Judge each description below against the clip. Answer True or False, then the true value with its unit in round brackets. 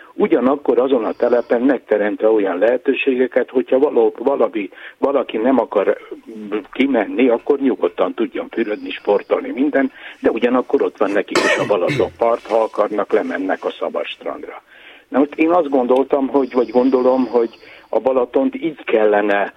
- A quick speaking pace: False (145 wpm)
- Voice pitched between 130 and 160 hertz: True (140 Hz)